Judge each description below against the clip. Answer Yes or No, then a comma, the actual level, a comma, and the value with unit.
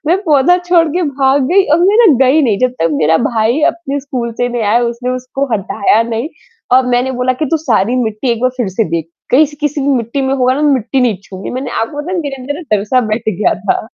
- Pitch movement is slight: No, average, 4.0 semitones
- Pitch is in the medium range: No, very high, 255 Hz